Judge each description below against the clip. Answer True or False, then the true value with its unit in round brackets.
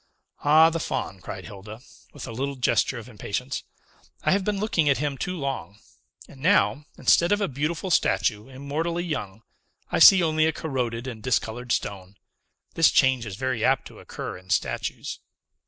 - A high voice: False (135 Hz)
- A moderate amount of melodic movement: False (6.0 semitones)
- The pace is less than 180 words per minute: True (170 wpm)